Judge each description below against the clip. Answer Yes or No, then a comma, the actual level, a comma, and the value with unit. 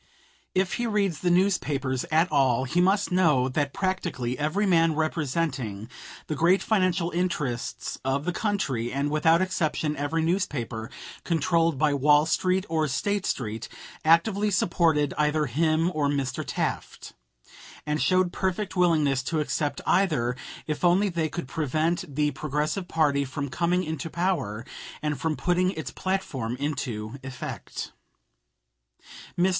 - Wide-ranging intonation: No, average, 4.2 semitones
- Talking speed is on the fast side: No, average, 140 wpm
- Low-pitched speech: No, medium, 155 Hz